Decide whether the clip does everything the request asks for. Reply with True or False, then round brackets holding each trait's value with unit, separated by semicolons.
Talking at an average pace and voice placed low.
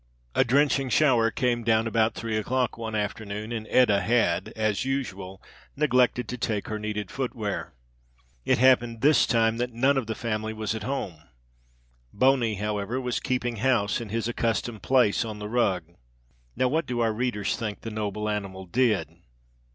True (165 wpm; 115 Hz)